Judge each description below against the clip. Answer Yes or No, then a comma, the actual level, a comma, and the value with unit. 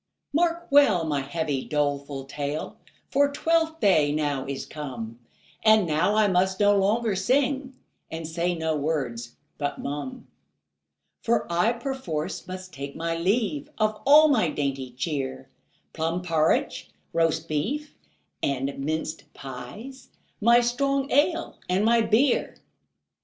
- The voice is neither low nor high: Yes, medium, 170 Hz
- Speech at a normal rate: No, slow, 130 wpm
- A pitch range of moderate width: No, wide, 8.5 semitones